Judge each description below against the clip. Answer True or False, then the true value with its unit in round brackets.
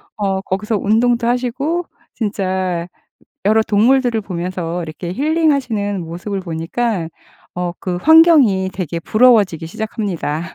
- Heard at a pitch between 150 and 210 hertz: True (205 Hz)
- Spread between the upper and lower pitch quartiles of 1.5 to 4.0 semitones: False (5.2 semitones)